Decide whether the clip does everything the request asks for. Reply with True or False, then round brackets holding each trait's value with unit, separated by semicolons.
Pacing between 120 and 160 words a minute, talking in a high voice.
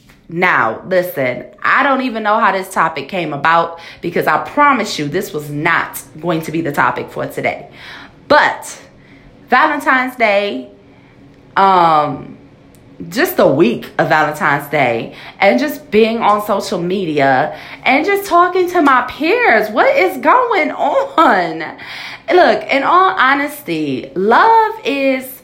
True (135 wpm; 205 Hz)